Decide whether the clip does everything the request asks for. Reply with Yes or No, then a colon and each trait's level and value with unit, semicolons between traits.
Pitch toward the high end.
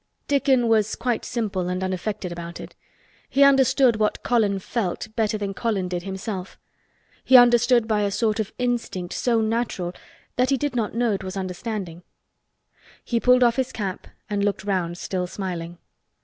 Yes: high, 215 Hz